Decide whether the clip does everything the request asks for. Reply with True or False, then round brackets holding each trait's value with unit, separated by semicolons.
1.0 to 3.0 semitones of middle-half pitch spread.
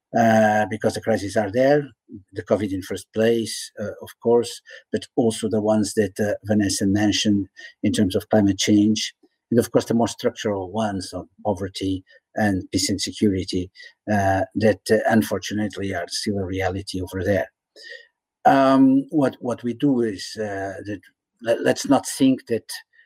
True (2.7 semitones)